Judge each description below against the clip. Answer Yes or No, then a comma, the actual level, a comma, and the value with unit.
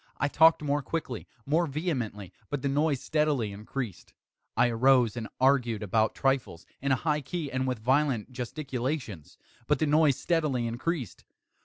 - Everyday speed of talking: Yes, average, 155 wpm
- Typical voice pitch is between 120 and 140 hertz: Yes, low, 135 Hz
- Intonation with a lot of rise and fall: No, average, 4.2 semitones